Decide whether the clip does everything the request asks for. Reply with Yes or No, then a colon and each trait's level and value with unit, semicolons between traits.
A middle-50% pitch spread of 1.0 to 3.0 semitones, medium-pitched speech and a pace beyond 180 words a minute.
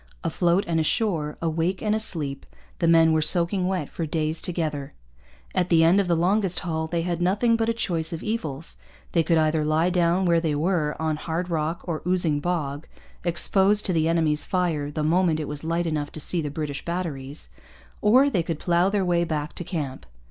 Yes: narrow, 2.6 semitones; medium, 165 Hz; average, 200 wpm